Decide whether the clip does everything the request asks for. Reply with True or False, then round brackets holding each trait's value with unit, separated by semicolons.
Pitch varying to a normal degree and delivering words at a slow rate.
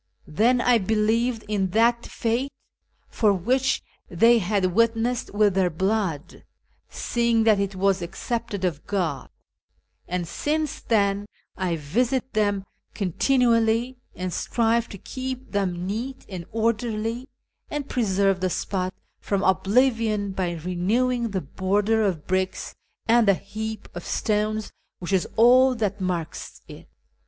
True (3.8 semitones; 130 wpm)